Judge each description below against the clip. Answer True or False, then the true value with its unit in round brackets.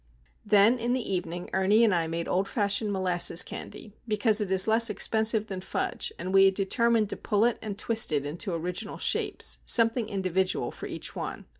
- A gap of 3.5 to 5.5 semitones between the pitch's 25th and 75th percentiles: False (3.1 semitones)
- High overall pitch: True (200 Hz)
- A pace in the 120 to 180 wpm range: False (190 wpm)